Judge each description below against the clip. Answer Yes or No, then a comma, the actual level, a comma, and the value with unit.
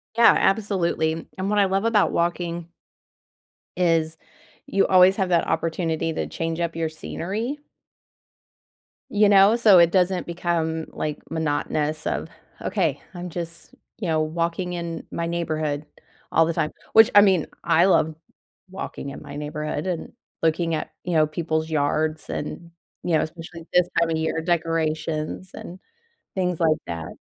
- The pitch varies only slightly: Yes, narrow, 2.2 semitones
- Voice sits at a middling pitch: Yes, medium, 165 Hz